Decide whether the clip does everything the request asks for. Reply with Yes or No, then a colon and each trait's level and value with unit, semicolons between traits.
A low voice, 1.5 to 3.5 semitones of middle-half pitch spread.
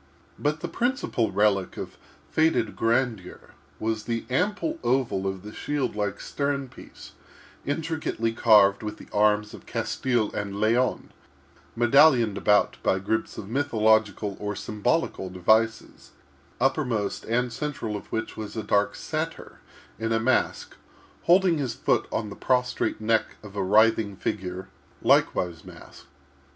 No: low, 110 Hz; average, 3.9 semitones